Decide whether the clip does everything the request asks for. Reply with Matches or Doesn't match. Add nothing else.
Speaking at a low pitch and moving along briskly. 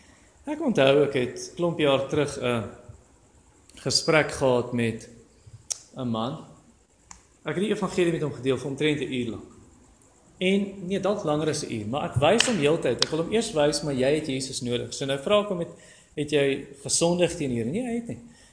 Doesn't match